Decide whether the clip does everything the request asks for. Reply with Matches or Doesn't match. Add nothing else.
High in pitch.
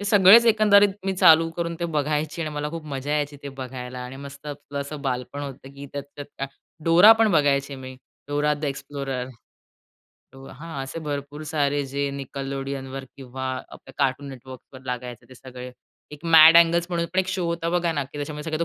Doesn't match